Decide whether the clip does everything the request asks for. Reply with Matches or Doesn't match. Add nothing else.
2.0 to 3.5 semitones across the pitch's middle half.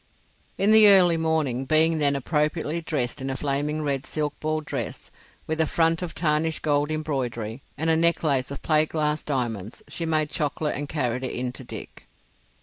Matches